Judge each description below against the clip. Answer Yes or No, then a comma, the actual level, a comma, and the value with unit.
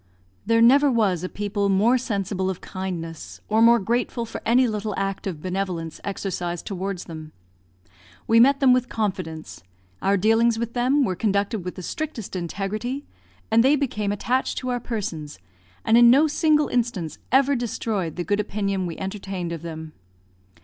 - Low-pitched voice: No, high, 205 Hz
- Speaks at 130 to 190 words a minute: Yes, average, 165 wpm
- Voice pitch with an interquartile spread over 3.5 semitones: Yes, average, 4.3 semitones